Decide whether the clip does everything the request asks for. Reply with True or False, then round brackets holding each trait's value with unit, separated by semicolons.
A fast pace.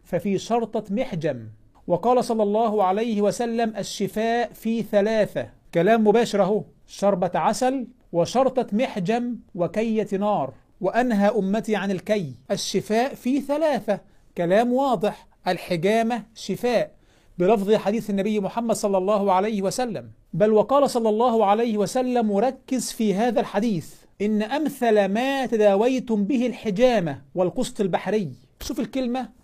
False (120 wpm)